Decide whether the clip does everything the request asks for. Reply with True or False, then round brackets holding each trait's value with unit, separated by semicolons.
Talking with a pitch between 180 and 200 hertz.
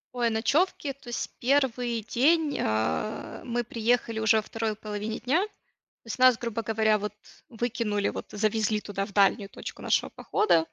False (225 Hz)